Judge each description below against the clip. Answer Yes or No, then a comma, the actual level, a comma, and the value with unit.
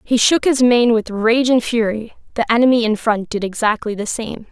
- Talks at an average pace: No, fast, 210 wpm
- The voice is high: Yes, high, 230 Hz